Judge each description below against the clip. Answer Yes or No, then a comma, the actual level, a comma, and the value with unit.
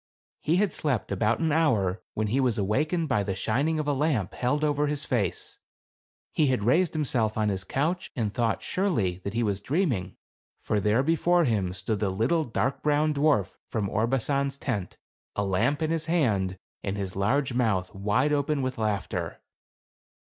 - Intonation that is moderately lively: No, wide, 6.5 semitones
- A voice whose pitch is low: Yes, low, 125 Hz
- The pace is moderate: Yes, average, 180 wpm